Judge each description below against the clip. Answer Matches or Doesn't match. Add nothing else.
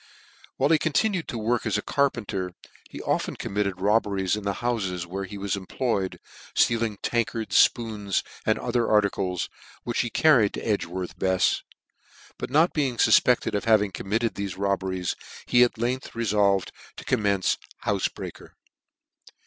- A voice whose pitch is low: Matches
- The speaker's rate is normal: Matches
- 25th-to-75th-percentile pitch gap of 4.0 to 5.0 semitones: Doesn't match